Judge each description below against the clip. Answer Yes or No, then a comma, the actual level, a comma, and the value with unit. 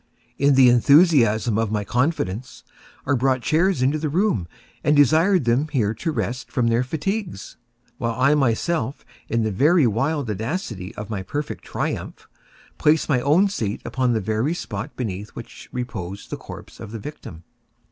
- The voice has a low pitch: Yes, low, 125 Hz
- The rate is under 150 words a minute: No, average, 160 wpm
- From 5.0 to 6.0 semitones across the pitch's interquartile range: Yes, wide, 5.4 semitones